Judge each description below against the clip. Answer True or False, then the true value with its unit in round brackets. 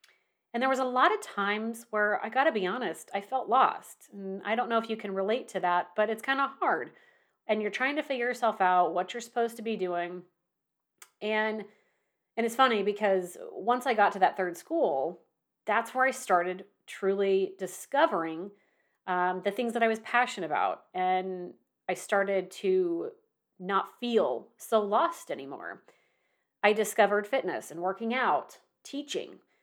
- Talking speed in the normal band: True (170 wpm)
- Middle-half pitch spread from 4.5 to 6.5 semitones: True (4.9 semitones)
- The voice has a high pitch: True (215 Hz)